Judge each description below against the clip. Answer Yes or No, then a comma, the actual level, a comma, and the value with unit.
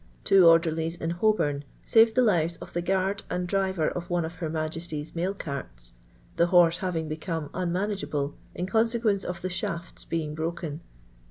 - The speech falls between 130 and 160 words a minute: No, average, 175 wpm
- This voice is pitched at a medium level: Yes, medium, 170 Hz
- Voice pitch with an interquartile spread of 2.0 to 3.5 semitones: Yes, average, 2.8 semitones